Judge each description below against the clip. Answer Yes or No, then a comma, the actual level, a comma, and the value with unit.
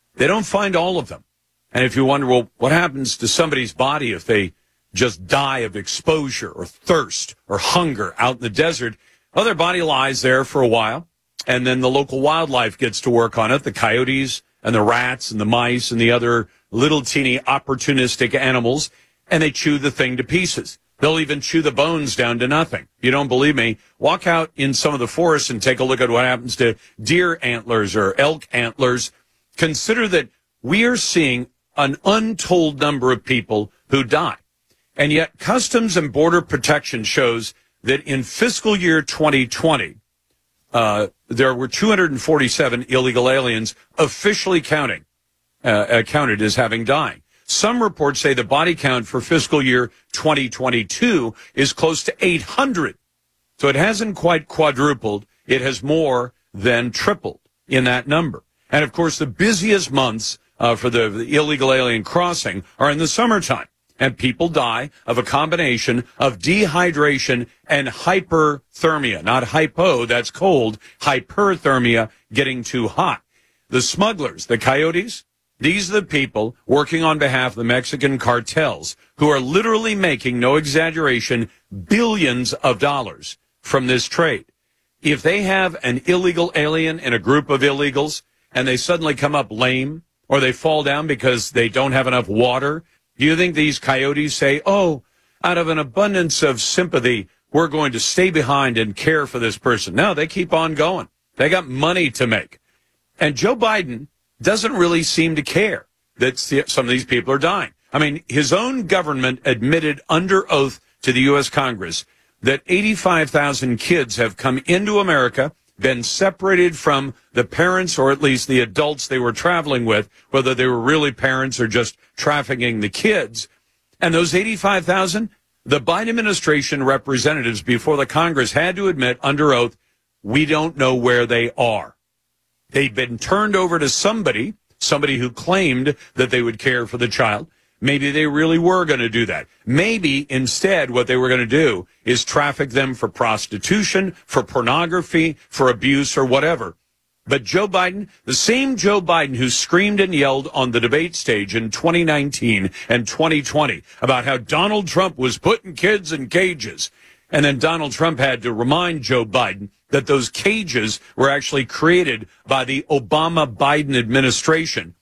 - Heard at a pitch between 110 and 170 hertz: Yes, medium, 140 Hz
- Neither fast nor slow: Yes, average, 165 wpm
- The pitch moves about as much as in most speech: Yes, average, 4.7 semitones